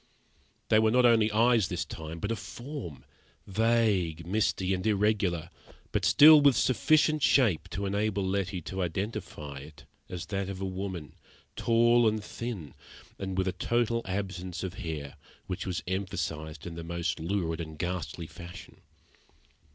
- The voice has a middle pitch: No, very low, 95 Hz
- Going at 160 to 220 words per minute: No, average, 150 wpm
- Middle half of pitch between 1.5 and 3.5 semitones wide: No, average, 4.4 semitones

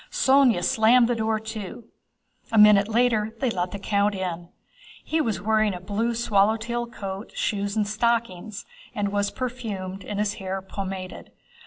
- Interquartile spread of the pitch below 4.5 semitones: Yes, average, 2.7 semitones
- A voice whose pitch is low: No, high, 210 Hz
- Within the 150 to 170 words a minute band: Yes, average, 160 wpm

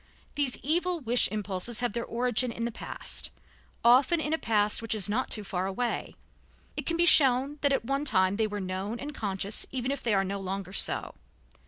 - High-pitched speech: Yes, high, 235 Hz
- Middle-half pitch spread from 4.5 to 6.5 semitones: Yes, average, 5.1 semitones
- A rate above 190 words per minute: Yes, fast, 205 wpm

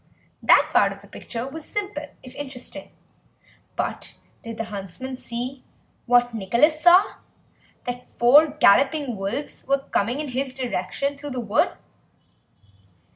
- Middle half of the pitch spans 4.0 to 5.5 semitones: No, average, 3.5 semitones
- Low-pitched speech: No, very high, 255 Hz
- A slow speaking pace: Yes, slow, 130 wpm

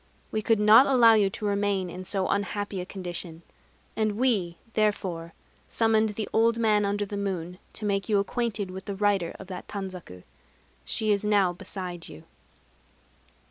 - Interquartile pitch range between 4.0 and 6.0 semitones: No, narrow, 2.6 semitones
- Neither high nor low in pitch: No, high, 200 Hz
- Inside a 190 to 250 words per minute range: No, average, 165 wpm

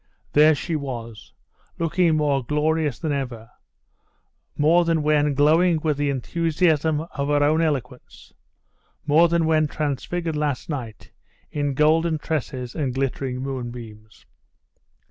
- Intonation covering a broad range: No, average, 3.1 semitones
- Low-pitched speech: No, medium, 150 Hz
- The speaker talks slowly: Yes, slow, 125 wpm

